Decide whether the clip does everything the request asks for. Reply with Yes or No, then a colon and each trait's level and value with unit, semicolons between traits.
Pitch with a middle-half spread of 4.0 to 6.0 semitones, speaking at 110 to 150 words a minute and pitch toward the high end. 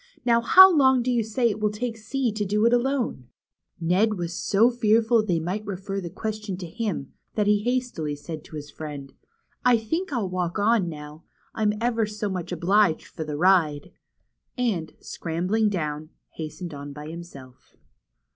No: wide, 5.6 semitones; average, 180 wpm; high, 205 Hz